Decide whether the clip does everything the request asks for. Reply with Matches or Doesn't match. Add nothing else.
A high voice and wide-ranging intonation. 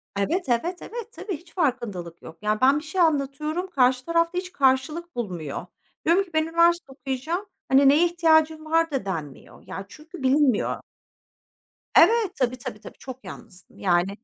Matches